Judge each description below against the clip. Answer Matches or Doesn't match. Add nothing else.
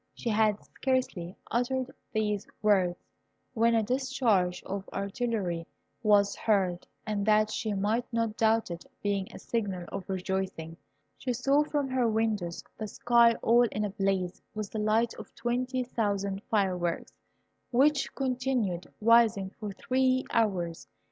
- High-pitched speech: Matches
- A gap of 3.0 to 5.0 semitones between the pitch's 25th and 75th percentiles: Matches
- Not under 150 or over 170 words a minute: Doesn't match